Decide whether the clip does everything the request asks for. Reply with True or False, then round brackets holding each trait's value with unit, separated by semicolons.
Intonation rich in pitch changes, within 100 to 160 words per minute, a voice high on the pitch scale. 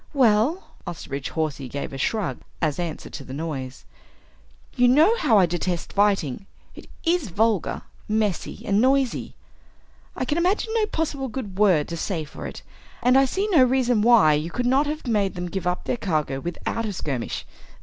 False (7.8 semitones; 180 wpm; 210 Hz)